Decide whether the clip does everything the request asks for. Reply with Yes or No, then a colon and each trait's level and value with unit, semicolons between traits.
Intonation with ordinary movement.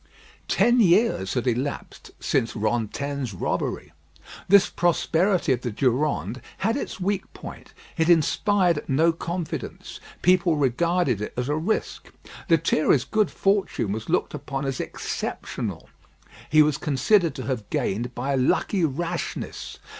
No: wide, 5.9 semitones